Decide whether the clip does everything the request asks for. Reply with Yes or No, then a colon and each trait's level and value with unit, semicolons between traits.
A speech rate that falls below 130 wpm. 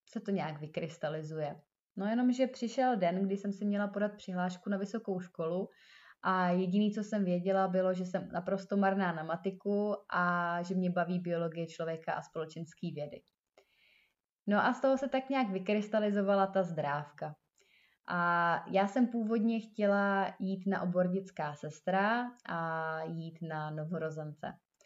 No: average, 150 wpm